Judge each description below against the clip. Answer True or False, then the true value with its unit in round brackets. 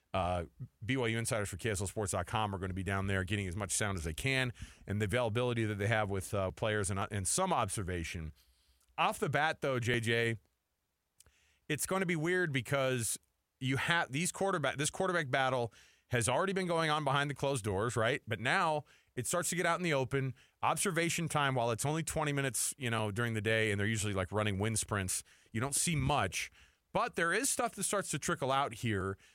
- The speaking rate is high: True (210 wpm)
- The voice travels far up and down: True (6.3 semitones)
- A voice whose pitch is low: True (120 Hz)